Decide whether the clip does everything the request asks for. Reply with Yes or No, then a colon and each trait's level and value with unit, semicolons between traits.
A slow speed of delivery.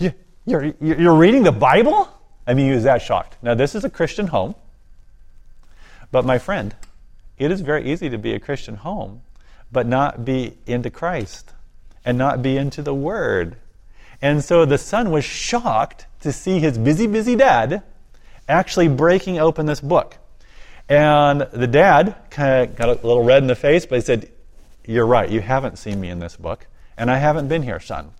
No: average, 185 wpm